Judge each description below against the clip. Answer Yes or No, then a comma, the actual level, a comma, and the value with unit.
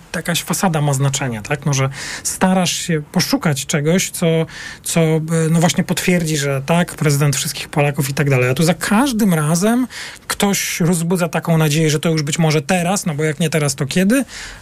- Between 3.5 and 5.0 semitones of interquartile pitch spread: No, average, 2.9 semitones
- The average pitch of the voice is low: No, medium, 165 Hz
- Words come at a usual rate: No, fast, 190 wpm